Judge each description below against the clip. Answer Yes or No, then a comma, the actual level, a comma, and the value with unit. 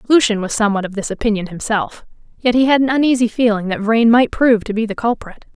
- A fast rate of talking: Yes, fast, 225 wpm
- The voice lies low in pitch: No, high, 225 Hz